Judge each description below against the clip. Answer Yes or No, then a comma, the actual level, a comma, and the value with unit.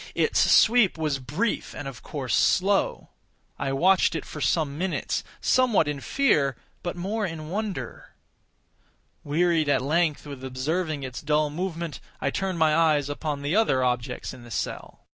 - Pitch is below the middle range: No, medium, 155 Hz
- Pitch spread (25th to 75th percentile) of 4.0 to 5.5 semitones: Yes, average, 4.4 semitones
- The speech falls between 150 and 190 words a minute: Yes, average, 160 wpm